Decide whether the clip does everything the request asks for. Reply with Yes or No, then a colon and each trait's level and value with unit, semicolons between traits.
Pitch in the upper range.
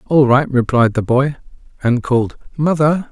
No: low, 135 Hz